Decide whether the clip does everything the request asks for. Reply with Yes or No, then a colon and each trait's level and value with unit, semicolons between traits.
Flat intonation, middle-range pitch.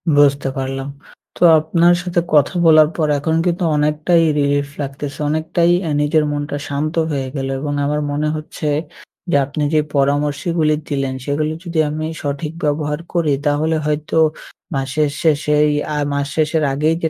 Yes: narrow, 1.7 semitones; medium, 150 Hz